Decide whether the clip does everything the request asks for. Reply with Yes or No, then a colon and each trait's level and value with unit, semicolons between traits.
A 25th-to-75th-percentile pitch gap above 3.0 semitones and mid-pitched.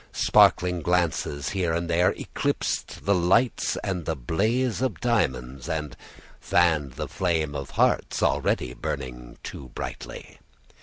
No: average, 4.8 semitones; very low, 85 Hz